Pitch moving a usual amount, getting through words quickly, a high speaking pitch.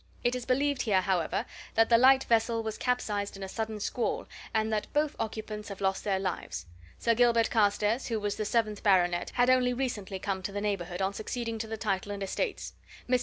Yes: average, 3.2 semitones; fast, 210 wpm; high, 215 Hz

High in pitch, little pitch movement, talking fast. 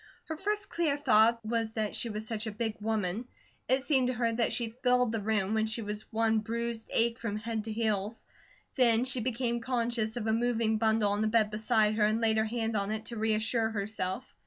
Yes: high, 225 Hz; narrow, 1.5 semitones; fast, 220 wpm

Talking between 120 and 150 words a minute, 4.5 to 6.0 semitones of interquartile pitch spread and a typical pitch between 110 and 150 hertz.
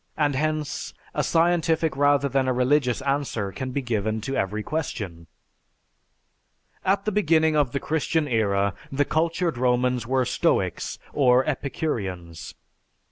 Yes: slow, 135 wpm; average, 4.8 semitones; low, 135 Hz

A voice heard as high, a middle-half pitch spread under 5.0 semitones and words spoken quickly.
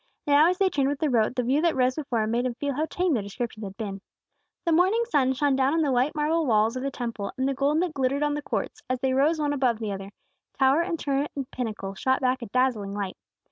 Yes: very high, 265 Hz; average, 3.9 semitones; fast, 265 wpm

